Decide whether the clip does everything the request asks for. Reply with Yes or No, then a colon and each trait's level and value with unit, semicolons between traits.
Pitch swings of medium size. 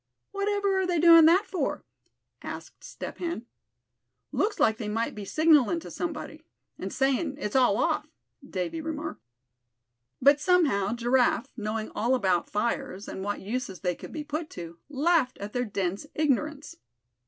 No: wide, 7.2 semitones